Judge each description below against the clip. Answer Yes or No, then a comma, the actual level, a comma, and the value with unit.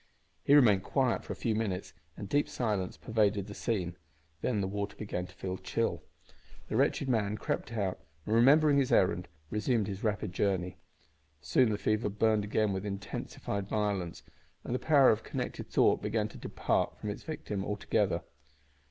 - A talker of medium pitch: No, low, 105 Hz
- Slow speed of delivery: No, average, 170 wpm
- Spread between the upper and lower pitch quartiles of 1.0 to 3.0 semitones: Yes, average, 2.7 semitones